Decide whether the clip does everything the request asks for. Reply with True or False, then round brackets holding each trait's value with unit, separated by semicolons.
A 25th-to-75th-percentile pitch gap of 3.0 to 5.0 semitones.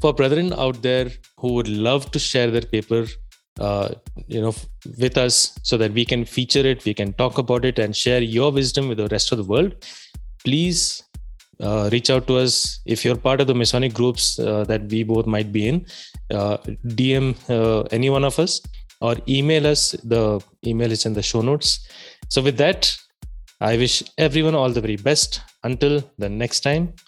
True (3.7 semitones)